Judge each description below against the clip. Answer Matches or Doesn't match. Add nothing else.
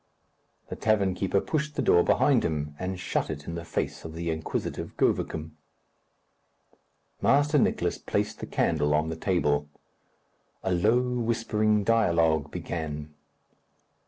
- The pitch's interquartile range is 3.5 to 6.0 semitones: Matches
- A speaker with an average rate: Doesn't match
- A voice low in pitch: Matches